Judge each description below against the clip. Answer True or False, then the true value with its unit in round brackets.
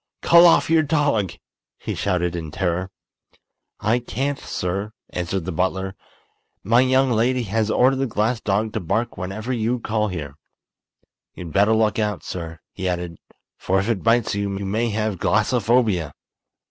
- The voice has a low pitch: True (105 Hz)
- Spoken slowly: False (160 wpm)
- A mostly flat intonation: False (4.2 semitones)